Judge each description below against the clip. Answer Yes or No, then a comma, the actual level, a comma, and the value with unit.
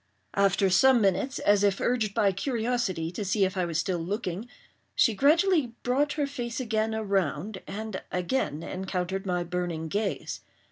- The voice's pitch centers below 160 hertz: No, high, 200 Hz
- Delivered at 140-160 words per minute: Yes, average, 155 wpm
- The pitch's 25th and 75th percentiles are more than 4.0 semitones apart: Yes, average, 4.6 semitones